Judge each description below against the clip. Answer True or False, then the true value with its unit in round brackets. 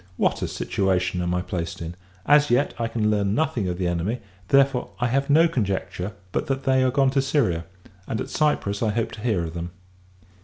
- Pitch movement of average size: False (6.9 semitones)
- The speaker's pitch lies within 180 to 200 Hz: False (110 Hz)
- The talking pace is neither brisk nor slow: False (215 wpm)